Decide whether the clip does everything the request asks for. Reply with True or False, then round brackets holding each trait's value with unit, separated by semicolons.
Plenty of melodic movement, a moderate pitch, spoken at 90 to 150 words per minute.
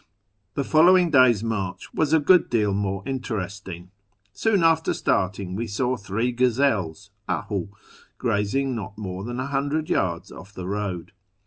False (5.9 semitones; 110 Hz; 145 wpm)